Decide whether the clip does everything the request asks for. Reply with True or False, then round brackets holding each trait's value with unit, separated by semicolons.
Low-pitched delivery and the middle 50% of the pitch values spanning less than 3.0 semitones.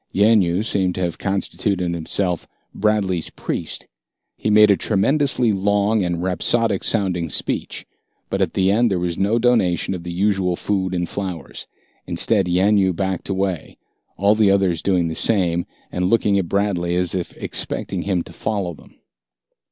True (95 Hz; 2.6 semitones)